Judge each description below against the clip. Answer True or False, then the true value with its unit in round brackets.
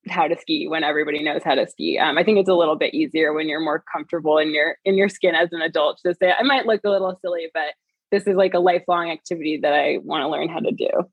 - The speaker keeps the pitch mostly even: False (3.9 semitones)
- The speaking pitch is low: False (175 Hz)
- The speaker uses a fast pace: True (280 wpm)